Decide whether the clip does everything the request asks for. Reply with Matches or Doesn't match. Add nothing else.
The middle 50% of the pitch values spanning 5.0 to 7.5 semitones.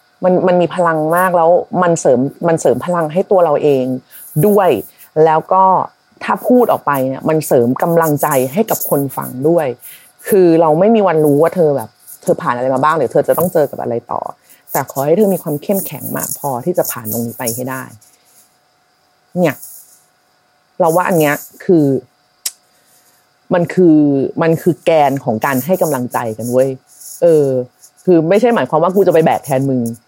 Matches